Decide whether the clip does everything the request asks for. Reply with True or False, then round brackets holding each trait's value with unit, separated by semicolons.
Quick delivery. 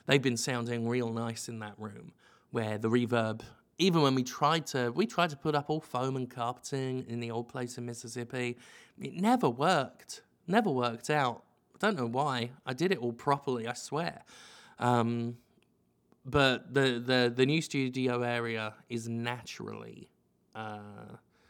False (165 wpm)